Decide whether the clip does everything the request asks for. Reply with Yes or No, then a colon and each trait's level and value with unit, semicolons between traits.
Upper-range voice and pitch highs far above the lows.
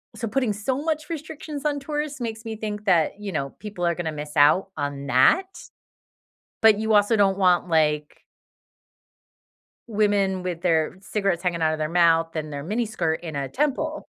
Yes: high, 195 Hz; wide, 5.9 semitones